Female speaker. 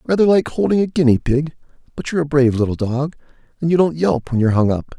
No: male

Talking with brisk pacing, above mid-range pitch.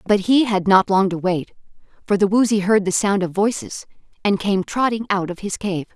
Yes: fast, 220 wpm; high, 200 Hz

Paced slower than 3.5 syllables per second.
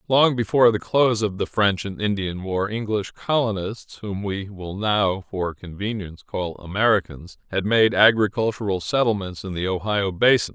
No: 4.9 syllables/s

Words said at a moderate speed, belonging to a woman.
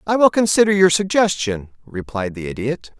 No: average, 160 wpm; male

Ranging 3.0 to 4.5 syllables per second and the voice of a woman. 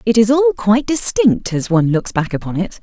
No: 5.8 syllables/s; female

